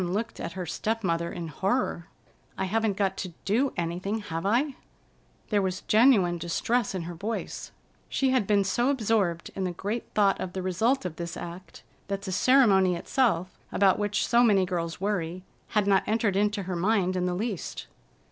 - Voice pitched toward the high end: Yes, high, 195 Hz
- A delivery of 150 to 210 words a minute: Yes, average, 185 wpm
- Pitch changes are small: No, average, 3.7 semitones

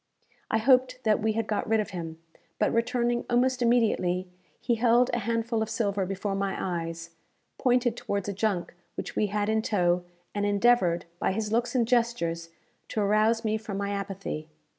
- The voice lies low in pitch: No, high, 215 Hz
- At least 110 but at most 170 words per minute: No, average, 180 wpm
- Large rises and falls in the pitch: No, average, 3.2 semitones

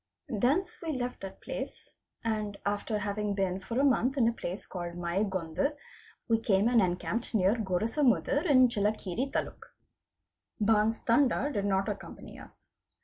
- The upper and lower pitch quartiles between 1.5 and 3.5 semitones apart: No, average, 4.1 semitones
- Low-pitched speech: No, high, 215 Hz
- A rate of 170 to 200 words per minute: No, average, 145 wpm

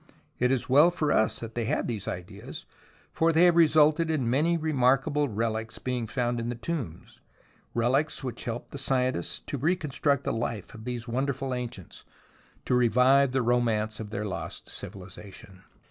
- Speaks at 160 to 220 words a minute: Yes, average, 165 wpm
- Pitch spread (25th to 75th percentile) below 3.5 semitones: No, average, 4.0 semitones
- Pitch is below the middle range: Yes, low, 125 Hz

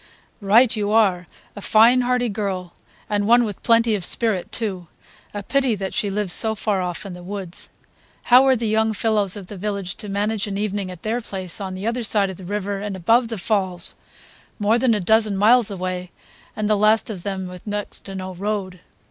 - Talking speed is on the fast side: Yes, fast, 210 wpm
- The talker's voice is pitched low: No, high, 205 Hz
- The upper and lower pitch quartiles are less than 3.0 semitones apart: Yes, narrow, 2.6 semitones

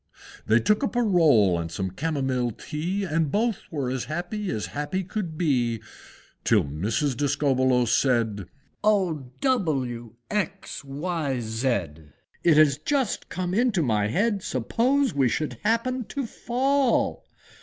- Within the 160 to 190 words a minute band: No, slow, 135 wpm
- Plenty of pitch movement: Yes, wide, 8.8 semitones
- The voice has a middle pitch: Yes, medium, 150 Hz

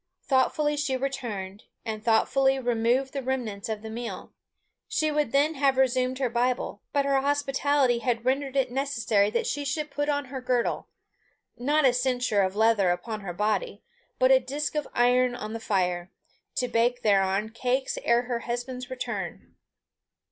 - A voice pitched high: Yes, very high, 250 Hz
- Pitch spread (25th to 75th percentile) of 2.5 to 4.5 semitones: Yes, average, 3.3 semitones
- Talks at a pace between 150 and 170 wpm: Yes, average, 165 wpm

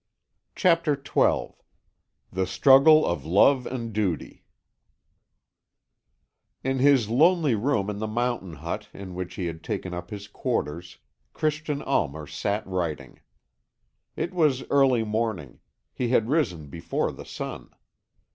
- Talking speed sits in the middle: No, slow, 125 wpm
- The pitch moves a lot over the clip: Yes, wide, 7.4 semitones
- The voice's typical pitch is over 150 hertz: No, low, 110 Hz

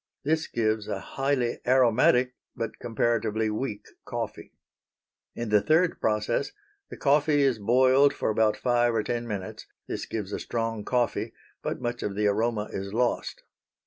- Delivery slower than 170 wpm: Yes, average, 150 wpm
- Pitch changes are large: No, average, 3.2 semitones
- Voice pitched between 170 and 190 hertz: No, low, 115 Hz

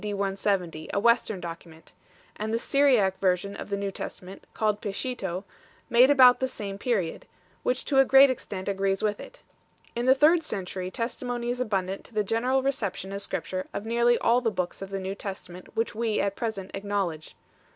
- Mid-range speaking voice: No, high, 205 Hz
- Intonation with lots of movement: No, average, 3.8 semitones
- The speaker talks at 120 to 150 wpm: No, average, 185 wpm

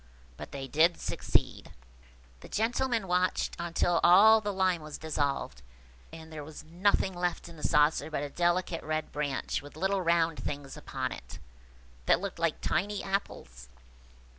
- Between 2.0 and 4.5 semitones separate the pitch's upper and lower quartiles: Yes, average, 3.9 semitones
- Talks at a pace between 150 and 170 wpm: Yes, average, 160 wpm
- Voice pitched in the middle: Yes, medium, 165 Hz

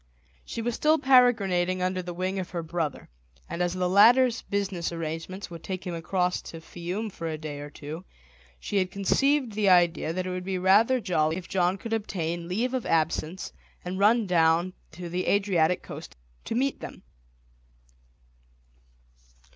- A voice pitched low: No, medium, 185 Hz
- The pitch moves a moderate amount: Yes, average, 3.1 semitones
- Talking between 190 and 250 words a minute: No, average, 170 wpm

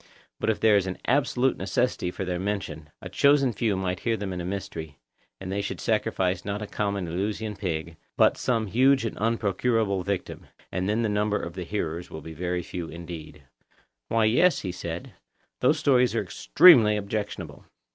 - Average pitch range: Yes, average, 3.9 semitones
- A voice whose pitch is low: Yes, low, 100 Hz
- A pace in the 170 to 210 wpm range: Yes, average, 185 wpm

